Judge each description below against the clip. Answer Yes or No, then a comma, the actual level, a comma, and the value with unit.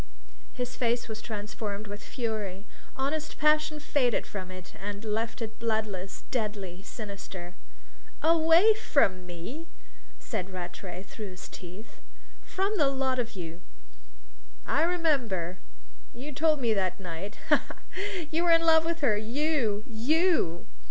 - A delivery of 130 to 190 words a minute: Yes, average, 140 wpm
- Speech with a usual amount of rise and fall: No, wide, 7.7 semitones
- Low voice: No, high, 225 Hz